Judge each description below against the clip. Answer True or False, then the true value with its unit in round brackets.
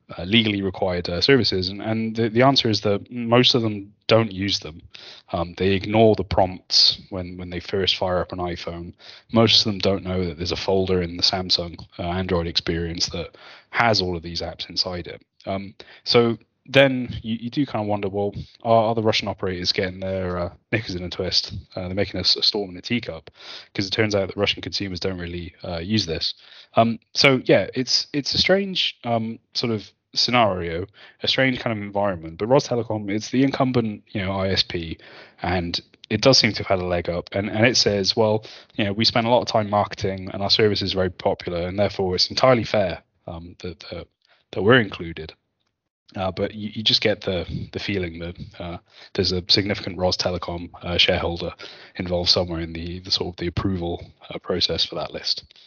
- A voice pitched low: True (100 Hz)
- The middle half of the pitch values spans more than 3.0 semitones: True (3.8 semitones)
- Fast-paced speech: True (210 wpm)